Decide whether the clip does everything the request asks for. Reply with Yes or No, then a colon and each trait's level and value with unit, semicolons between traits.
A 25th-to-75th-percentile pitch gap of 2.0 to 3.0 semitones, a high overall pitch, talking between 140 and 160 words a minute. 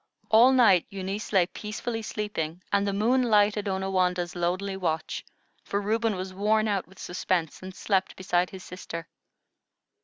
Yes: narrow, 2.6 semitones; high, 195 Hz; average, 150 wpm